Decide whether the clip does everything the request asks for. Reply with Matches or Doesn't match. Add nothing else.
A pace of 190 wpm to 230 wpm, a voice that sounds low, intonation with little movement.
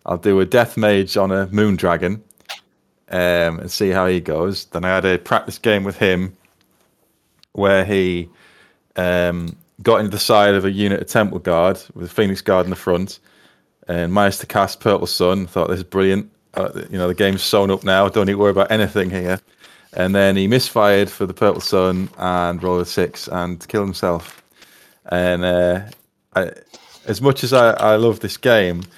Matches